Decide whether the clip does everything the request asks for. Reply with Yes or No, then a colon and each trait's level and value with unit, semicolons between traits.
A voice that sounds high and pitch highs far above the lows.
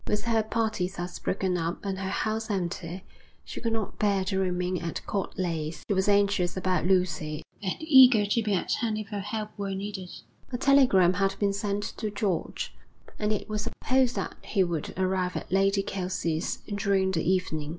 No: high, 195 Hz; narrow, 2.5 semitones